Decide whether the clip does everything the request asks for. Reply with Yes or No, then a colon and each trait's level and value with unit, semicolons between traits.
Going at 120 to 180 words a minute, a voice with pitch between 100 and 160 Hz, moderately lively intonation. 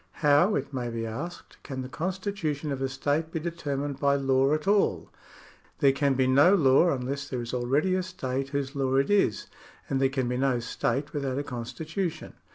No: average, 195 wpm; medium, 140 Hz; average, 3.0 semitones